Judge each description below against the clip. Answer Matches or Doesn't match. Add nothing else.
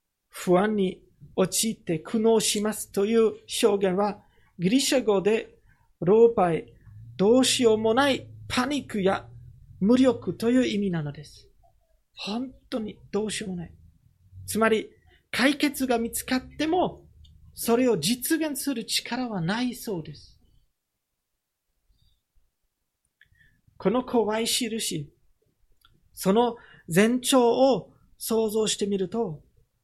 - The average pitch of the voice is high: Matches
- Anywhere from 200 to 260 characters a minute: Matches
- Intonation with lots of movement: Doesn't match